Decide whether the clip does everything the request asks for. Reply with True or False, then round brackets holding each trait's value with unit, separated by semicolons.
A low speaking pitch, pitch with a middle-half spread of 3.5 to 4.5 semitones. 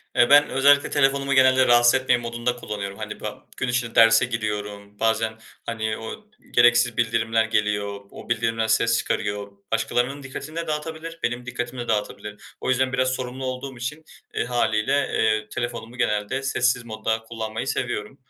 False (120 Hz; 2.8 semitones)